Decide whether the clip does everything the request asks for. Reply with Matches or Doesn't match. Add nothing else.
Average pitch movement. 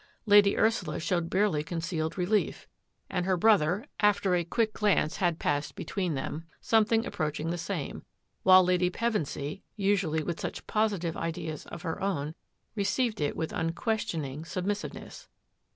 Matches